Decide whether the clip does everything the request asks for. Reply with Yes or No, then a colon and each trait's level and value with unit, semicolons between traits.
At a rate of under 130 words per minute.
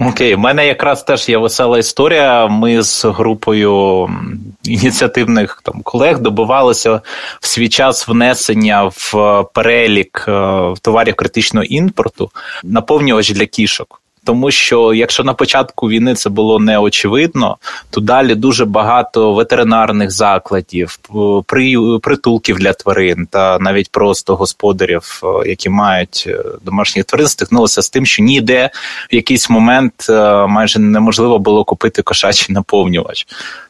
Yes: average, 120 wpm